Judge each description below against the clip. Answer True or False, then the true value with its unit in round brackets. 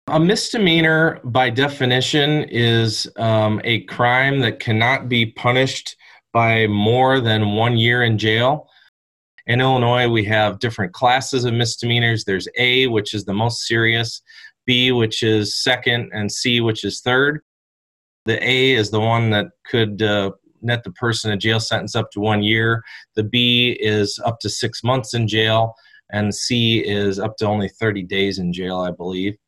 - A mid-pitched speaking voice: False (115 Hz)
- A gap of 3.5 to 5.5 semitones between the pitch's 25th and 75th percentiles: False (2.7 semitones)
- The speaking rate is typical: True (165 wpm)